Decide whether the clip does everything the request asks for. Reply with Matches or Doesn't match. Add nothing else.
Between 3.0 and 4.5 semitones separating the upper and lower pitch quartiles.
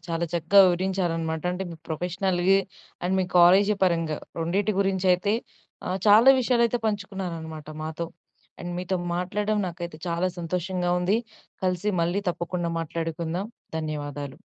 Doesn't match